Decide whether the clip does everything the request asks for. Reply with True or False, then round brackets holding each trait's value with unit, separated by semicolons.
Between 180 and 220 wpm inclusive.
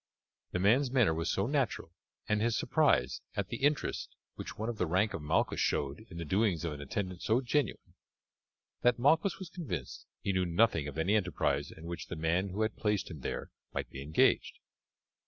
True (195 wpm)